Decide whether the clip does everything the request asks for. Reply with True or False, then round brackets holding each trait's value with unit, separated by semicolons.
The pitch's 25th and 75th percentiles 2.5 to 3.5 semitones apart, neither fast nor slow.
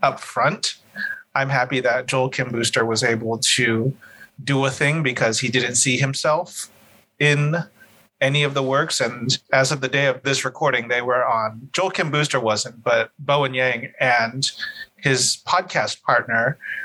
True (2.8 semitones; 165 wpm)